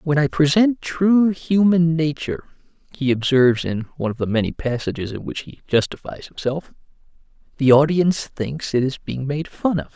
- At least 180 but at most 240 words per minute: No, average, 170 wpm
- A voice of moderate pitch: Yes, medium, 150 Hz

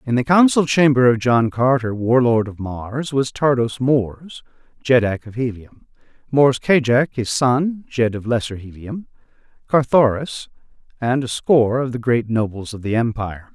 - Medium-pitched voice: No, low, 125 Hz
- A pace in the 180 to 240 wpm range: No, average, 155 wpm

